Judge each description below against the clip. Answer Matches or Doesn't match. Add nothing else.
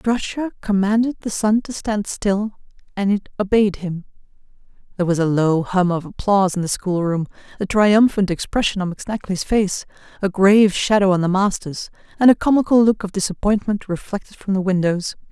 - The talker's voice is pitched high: Matches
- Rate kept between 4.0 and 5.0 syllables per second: Doesn't match